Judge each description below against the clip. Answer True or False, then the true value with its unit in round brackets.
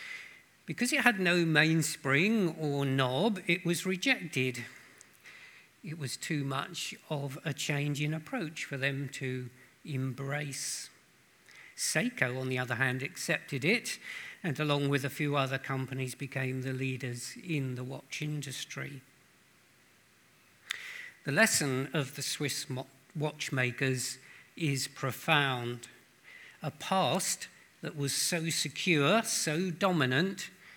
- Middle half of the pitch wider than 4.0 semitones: False (3.7 semitones)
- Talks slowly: True (115 wpm)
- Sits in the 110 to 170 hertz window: True (140 Hz)